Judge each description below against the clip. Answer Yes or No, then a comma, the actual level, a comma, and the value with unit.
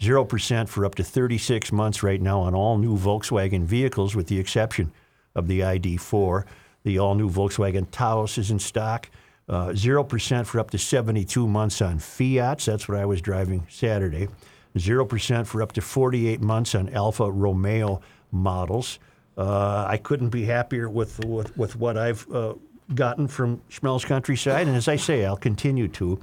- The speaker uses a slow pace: No, average, 170 wpm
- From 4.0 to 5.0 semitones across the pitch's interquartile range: No, average, 3.5 semitones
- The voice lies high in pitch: No, low, 110 Hz